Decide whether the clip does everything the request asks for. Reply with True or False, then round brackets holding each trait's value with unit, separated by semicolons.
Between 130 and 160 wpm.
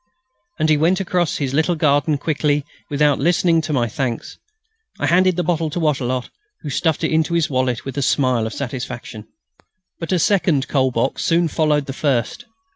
False (185 wpm)